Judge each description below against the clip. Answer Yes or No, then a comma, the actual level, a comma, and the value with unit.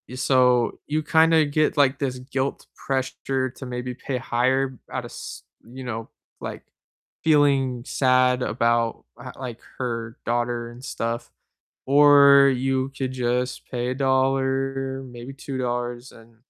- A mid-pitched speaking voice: No, low, 130 Hz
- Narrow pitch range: Yes, narrow, 1.7 semitones